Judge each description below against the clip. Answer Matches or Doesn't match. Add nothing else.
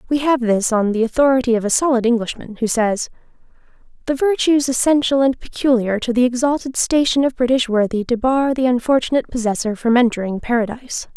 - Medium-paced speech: Matches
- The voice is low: Doesn't match